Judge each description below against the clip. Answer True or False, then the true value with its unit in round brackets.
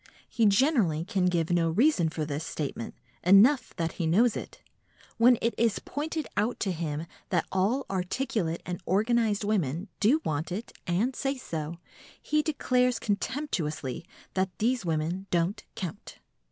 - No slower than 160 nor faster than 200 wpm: False (150 wpm)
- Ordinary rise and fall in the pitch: False (6.1 semitones)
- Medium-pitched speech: False (195 Hz)